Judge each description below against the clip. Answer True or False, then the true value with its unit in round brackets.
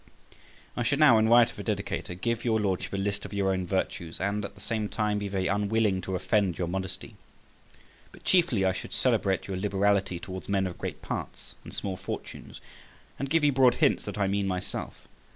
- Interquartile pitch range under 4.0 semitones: True (2.8 semitones)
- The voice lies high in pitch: False (100 Hz)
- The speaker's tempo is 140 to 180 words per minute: False (205 wpm)